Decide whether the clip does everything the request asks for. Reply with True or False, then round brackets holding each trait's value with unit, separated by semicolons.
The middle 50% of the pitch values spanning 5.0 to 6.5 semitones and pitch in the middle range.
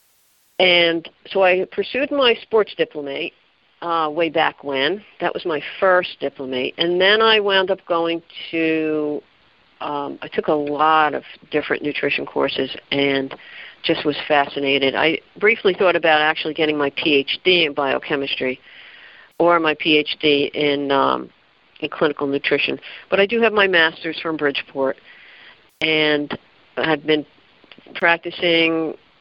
False (3.3 semitones; 155 Hz)